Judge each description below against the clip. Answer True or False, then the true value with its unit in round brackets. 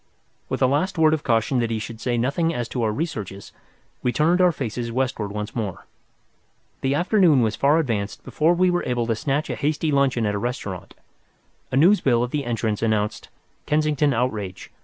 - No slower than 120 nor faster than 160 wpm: False (195 wpm)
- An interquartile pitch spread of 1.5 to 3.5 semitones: False (5.3 semitones)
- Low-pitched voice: True (125 Hz)